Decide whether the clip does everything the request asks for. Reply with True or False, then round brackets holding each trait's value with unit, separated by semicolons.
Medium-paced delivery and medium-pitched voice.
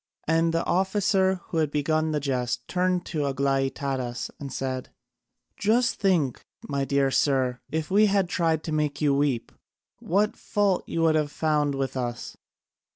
True (155 wpm; 150 Hz)